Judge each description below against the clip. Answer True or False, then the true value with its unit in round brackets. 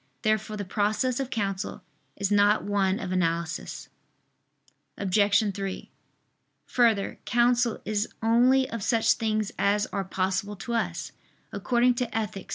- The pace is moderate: False (130 wpm)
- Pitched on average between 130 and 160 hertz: False (210 Hz)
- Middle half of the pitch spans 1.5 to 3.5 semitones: True (2.8 semitones)